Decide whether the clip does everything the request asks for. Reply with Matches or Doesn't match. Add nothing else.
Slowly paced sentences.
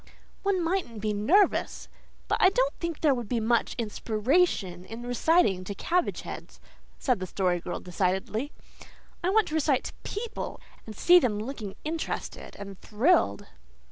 Doesn't match